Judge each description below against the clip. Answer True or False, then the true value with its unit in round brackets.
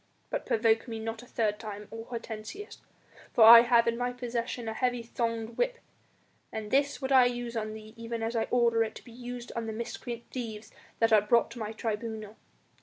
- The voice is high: True (230 Hz)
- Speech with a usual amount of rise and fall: False (1.6 semitones)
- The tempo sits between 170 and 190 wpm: False (205 wpm)